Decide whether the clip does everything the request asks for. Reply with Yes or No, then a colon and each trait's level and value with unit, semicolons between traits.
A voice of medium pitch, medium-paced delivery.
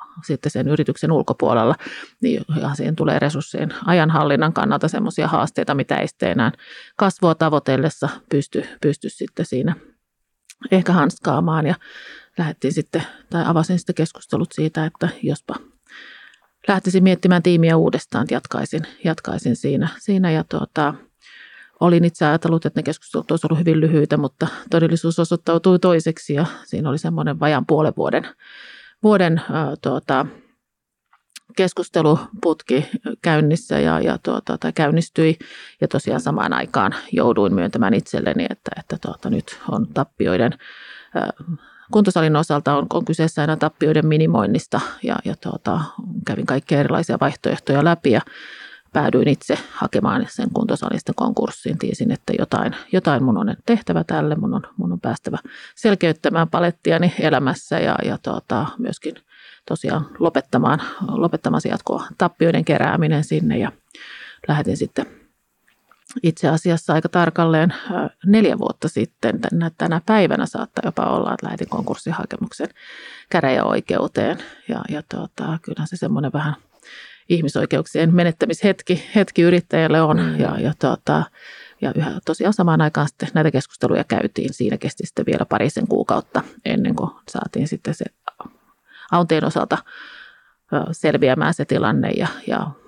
Yes: medium, 165 Hz; average, 125 wpm